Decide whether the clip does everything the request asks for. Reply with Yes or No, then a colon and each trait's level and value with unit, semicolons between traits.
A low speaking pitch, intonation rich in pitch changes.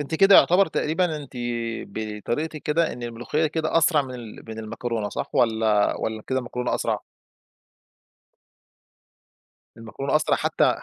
Yes: low, 130 Hz; wide, 5.8 semitones